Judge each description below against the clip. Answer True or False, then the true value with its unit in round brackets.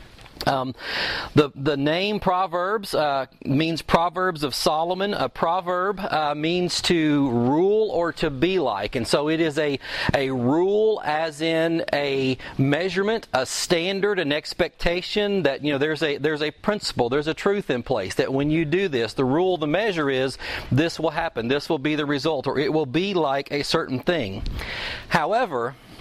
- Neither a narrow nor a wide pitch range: True (3.9 semitones)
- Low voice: False (160 Hz)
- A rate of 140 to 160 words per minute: False (175 wpm)